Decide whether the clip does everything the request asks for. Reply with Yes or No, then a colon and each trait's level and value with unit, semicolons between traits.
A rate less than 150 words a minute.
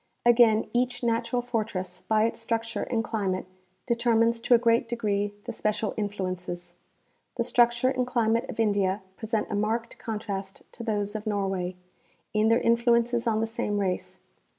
No: average, 165 wpm